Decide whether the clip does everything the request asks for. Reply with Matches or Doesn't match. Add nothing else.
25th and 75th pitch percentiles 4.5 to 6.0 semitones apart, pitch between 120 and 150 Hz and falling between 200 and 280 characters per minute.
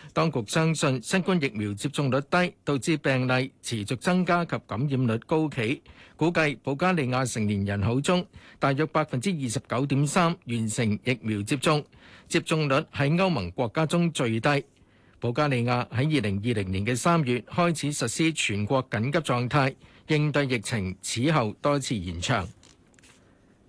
Matches